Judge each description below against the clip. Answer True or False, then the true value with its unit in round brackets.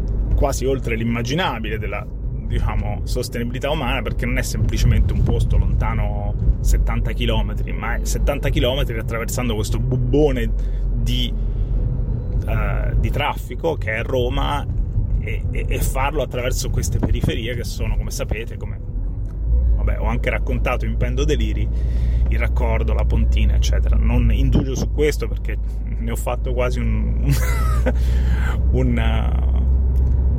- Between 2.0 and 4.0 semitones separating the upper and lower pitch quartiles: False (5.5 semitones)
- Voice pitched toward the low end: True (110 Hz)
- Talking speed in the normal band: True (130 wpm)